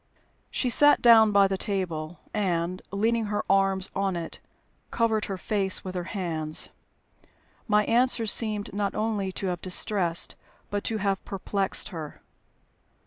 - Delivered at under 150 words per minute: Yes, average, 140 wpm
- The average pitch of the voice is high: Yes, high, 195 Hz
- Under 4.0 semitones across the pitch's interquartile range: Yes, narrow, 2.6 semitones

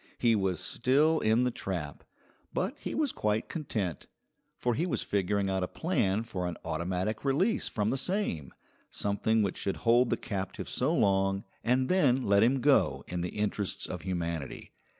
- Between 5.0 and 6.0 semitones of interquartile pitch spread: Yes, wide, 5.5 semitones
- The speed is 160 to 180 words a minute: Yes, average, 170 wpm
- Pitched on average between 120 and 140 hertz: No, low, 105 Hz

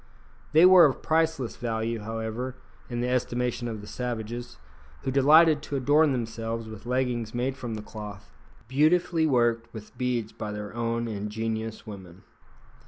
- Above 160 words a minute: No, average, 150 wpm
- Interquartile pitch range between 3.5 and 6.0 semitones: No, average, 2.9 semitones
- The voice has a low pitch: Yes, low, 120 Hz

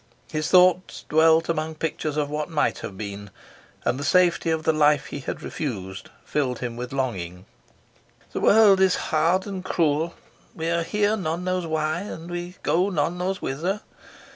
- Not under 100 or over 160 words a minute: No, average, 170 wpm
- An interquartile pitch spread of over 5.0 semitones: No, average, 3.8 semitones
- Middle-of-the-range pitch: Yes, medium, 160 Hz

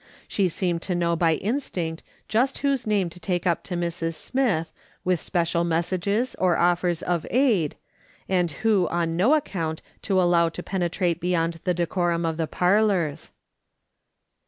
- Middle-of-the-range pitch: Yes, medium, 175 Hz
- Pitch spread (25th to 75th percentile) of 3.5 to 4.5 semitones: No, narrow, 2.5 semitones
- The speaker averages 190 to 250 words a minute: No, average, 155 wpm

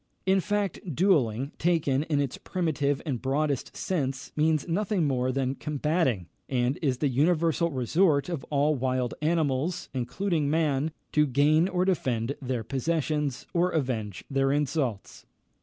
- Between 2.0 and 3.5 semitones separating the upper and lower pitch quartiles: No, average, 4.0 semitones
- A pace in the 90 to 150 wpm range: Yes, average, 140 wpm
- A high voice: No, medium, 145 Hz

